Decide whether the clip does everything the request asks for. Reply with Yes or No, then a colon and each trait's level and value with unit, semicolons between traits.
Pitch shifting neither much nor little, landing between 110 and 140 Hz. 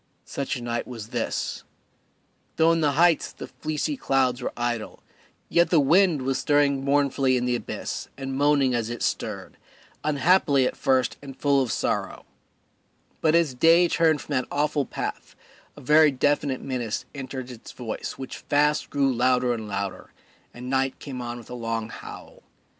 Yes: average, 3.0 semitones; low, 135 Hz